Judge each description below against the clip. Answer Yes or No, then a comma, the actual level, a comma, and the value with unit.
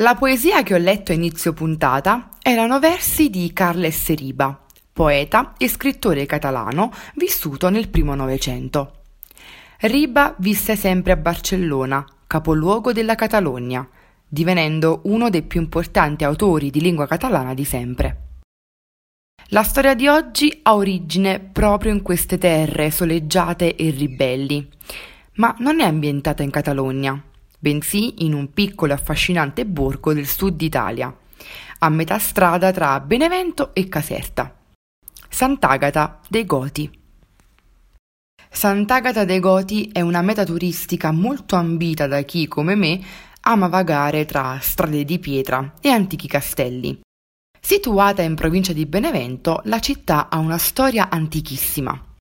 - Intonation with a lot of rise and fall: Yes, wide, 6.1 semitones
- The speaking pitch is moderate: Yes, medium, 170 Hz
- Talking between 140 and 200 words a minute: No, average, 130 wpm